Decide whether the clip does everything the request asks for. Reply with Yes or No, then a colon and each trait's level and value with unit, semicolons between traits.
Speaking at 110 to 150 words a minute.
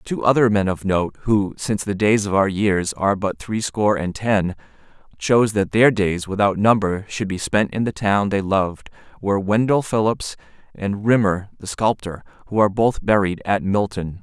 No: average, 185 wpm